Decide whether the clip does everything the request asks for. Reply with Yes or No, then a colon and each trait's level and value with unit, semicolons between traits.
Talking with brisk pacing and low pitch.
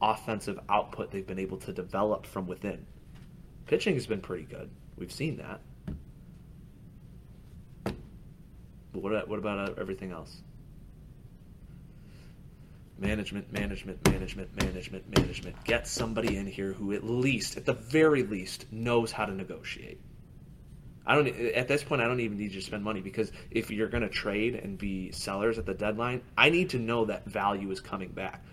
No: average, 165 wpm; low, 105 Hz